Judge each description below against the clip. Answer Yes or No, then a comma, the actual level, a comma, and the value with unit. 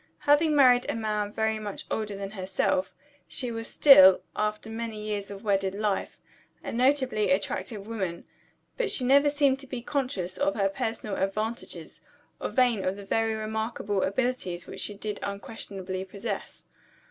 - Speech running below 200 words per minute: Yes, average, 160 wpm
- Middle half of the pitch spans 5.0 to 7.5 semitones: No, average, 4.0 semitones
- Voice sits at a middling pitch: No, high, 215 Hz